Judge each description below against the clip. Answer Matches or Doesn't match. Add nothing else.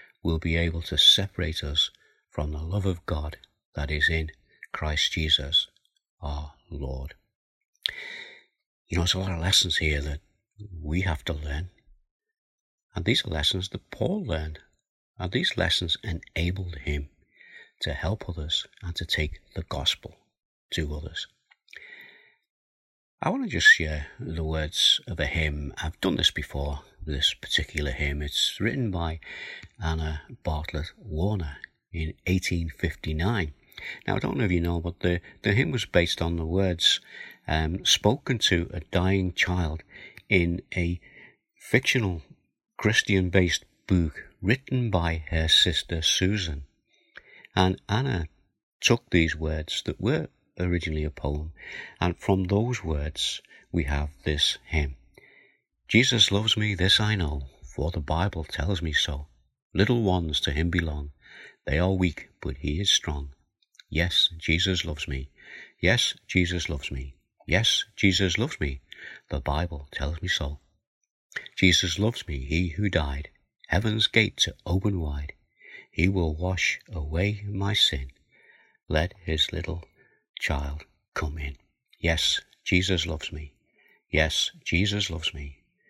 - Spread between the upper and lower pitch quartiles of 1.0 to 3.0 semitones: Doesn't match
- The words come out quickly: Doesn't match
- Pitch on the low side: Matches